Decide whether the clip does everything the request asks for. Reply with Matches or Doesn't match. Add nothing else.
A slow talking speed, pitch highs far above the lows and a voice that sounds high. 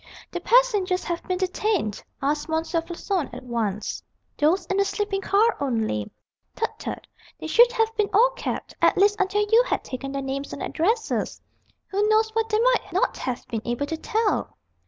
Doesn't match